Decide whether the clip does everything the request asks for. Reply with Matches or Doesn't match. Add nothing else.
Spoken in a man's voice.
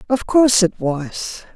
Doesn't match